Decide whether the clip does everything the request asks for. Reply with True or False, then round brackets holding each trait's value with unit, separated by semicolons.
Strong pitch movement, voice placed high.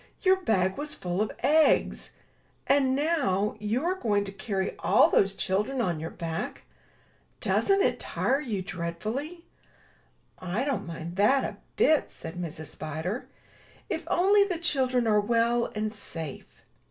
True (7.4 semitones; 215 Hz)